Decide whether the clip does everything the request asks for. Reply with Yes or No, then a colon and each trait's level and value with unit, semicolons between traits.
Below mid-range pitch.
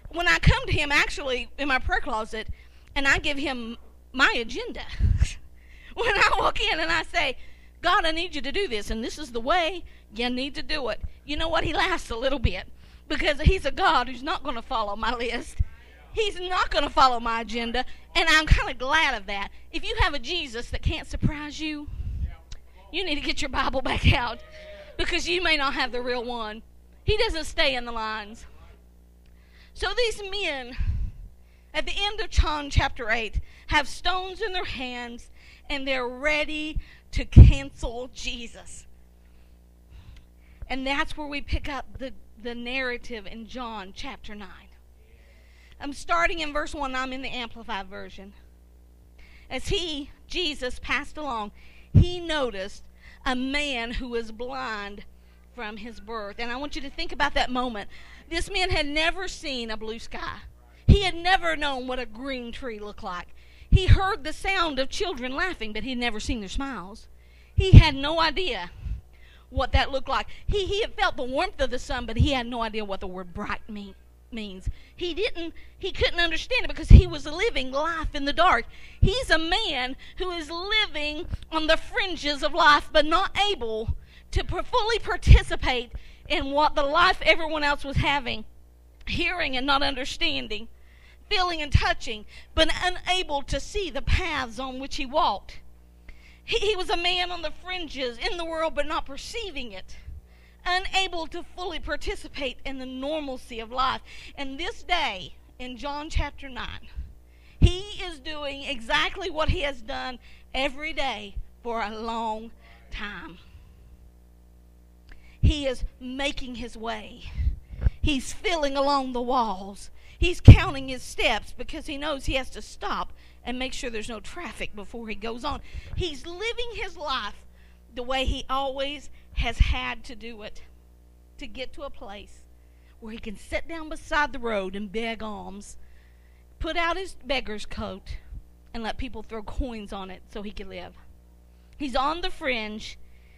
No: very high, 260 Hz